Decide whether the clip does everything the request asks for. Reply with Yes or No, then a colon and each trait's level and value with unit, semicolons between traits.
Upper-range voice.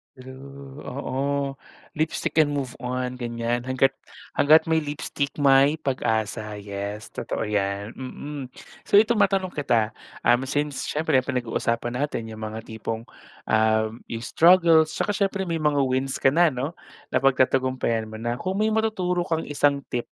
No: low, 135 Hz